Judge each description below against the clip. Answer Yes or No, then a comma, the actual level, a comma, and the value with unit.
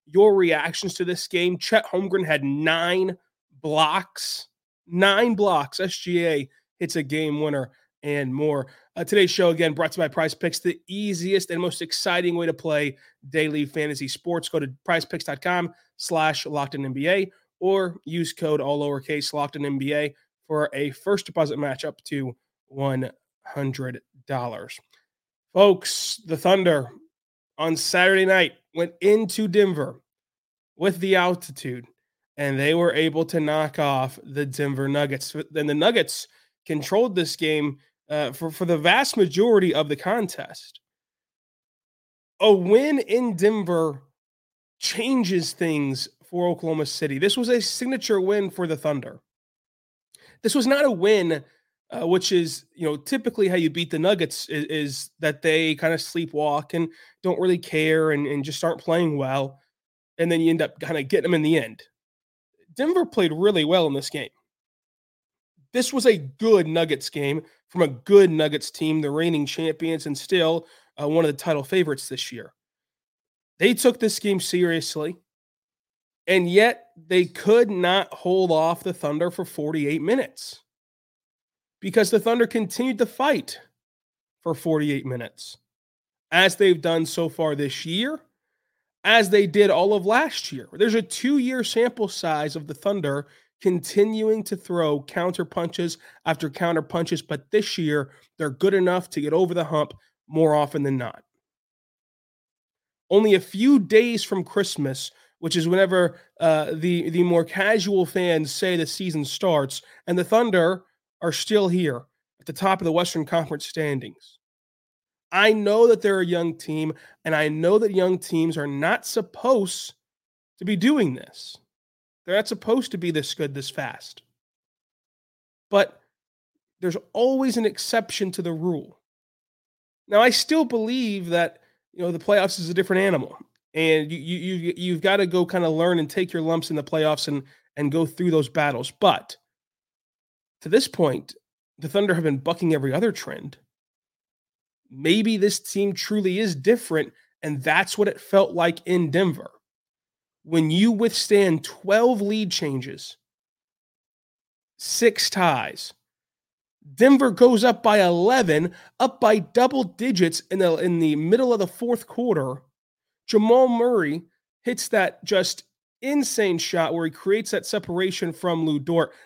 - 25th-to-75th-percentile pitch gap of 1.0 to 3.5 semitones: No, average, 4.7 semitones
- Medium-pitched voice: Yes, medium, 170 Hz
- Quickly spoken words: No, average, 155 wpm